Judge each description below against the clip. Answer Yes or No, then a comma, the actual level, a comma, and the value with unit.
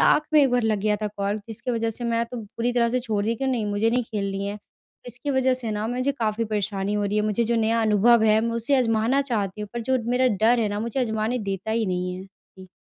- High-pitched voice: Yes, high, 225 Hz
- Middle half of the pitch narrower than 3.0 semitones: Yes, narrow, 2.6 semitones